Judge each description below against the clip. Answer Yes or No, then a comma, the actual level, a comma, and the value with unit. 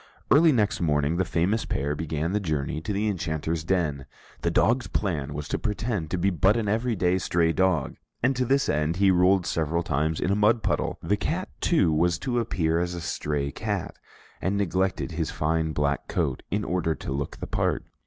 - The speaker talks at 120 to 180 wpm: No, average, 200 wpm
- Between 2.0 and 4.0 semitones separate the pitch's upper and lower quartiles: No, average, 4.6 semitones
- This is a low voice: Yes, very low, 90 Hz